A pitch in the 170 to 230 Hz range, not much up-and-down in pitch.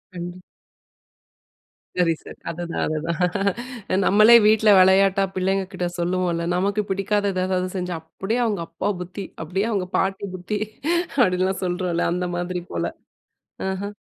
Yes: medium, 185 Hz; narrow, 1.9 semitones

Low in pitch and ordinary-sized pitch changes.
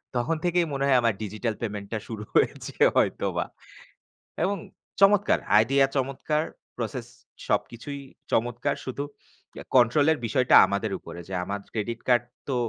Yes: low, 125 Hz; average, 4.2 semitones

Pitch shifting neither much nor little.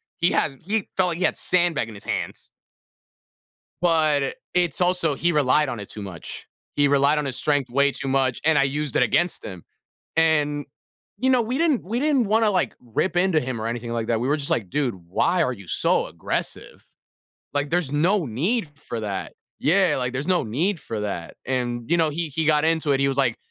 No: wide, 5.8 semitones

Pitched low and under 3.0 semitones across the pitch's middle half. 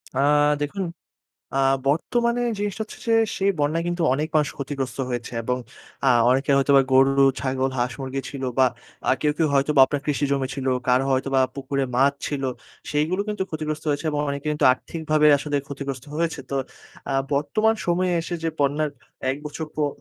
No: medium, 145 Hz; narrow, 2.6 semitones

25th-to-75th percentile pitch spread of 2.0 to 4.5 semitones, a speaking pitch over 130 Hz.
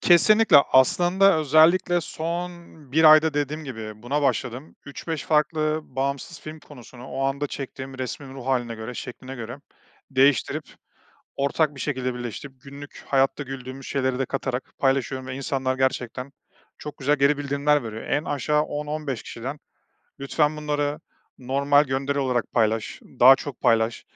Yes: narrow, 2.5 semitones; medium, 140 Hz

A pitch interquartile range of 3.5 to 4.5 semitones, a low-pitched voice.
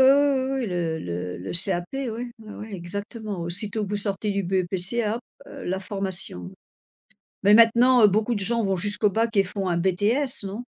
No: average, 3.8 semitones; high, 205 Hz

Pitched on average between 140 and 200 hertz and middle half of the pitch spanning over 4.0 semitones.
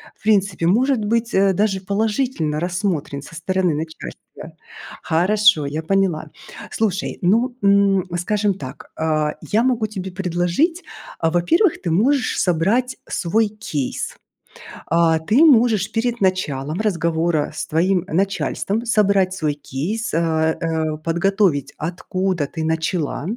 Yes: medium, 185 Hz; average, 4.7 semitones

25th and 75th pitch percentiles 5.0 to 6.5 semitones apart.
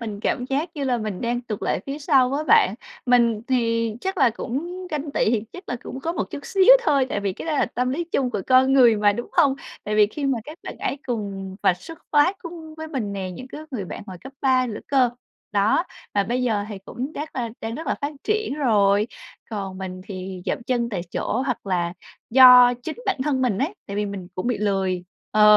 Yes: wide, 5.4 semitones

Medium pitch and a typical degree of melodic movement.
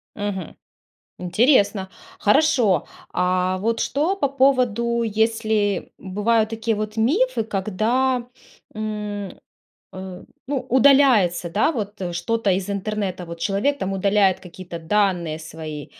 No: high, 210 Hz; average, 3.9 semitones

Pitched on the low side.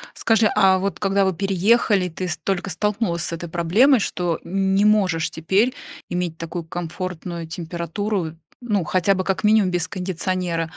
No: medium, 185 Hz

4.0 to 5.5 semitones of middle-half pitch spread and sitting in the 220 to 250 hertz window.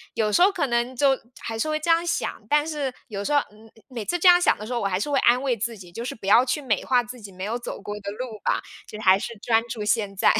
Yes: average, 4.7 semitones; high, 235 Hz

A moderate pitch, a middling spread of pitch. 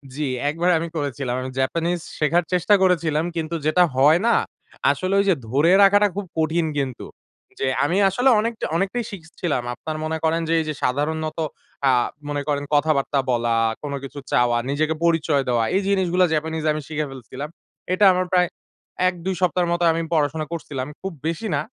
Yes: medium, 160 Hz; average, 3.6 semitones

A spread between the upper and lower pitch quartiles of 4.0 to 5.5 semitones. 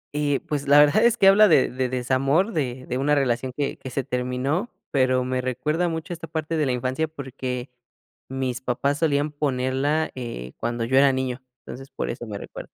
No: average, 2.9 semitones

